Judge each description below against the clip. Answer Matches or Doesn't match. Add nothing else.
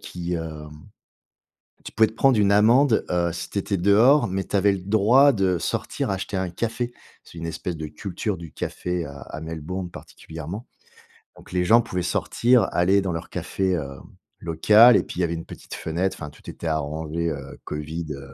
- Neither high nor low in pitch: Doesn't match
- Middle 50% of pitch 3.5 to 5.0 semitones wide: Matches